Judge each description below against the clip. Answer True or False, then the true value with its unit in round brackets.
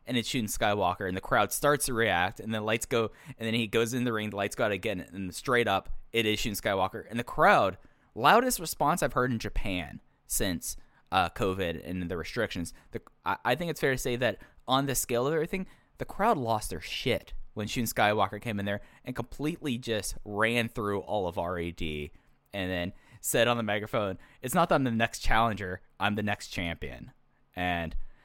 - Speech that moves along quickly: True (210 wpm)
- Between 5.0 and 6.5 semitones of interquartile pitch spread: False (4.3 semitones)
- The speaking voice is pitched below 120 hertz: True (110 Hz)